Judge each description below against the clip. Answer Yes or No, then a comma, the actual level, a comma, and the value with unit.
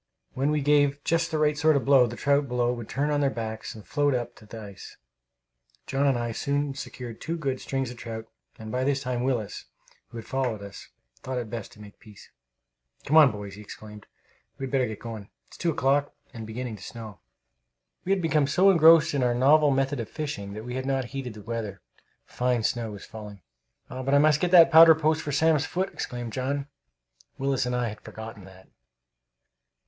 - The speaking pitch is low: Yes, low, 130 Hz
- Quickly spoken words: Yes, fast, 210 wpm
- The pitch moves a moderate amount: Yes, average, 4.3 semitones